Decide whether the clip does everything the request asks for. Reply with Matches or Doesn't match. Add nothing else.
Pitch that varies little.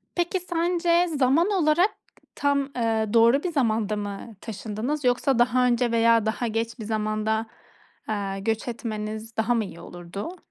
Doesn't match